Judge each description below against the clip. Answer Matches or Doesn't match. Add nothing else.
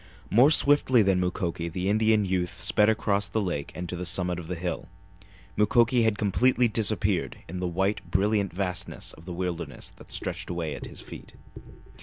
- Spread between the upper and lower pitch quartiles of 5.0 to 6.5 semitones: Doesn't match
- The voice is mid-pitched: Doesn't match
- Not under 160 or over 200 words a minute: Matches